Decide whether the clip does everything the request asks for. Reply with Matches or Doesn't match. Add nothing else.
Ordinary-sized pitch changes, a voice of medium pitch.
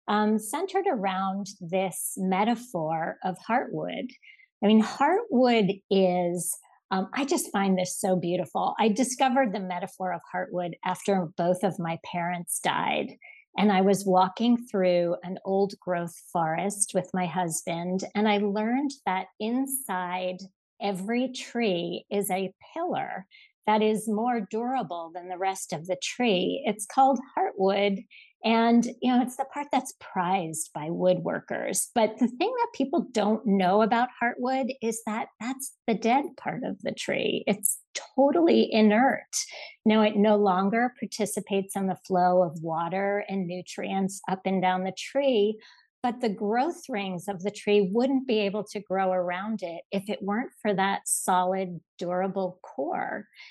Doesn't match